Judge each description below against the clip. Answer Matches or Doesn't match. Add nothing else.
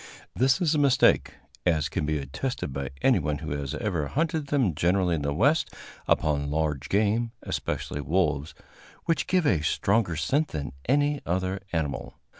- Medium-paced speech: Matches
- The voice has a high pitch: Doesn't match